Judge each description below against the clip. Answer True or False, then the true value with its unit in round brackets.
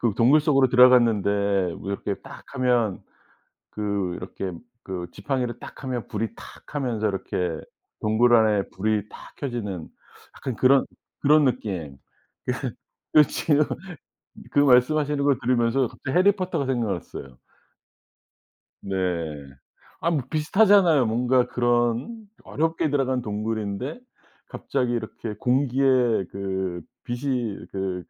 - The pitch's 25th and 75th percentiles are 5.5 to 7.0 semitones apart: False (5.1 semitones)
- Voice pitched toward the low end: True (120 Hz)